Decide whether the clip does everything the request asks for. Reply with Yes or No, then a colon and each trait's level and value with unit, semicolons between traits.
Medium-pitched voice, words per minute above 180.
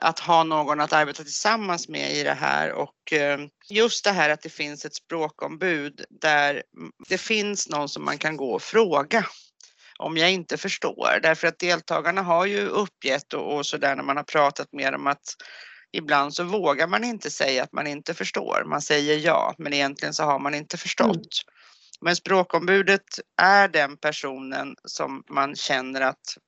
No: medium, 155 Hz; average, 175 wpm